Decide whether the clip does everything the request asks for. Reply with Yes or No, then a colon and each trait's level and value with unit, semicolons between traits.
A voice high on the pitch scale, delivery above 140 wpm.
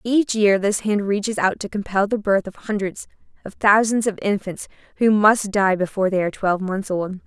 Yes: high, 200 Hz; fast, 205 wpm